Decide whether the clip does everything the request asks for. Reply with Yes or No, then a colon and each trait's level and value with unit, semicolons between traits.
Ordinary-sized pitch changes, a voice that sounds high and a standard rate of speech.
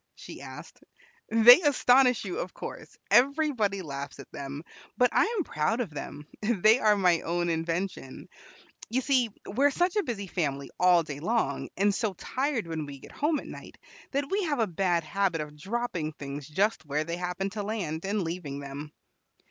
No: wide, 7.7 semitones; high, 195 Hz; average, 185 wpm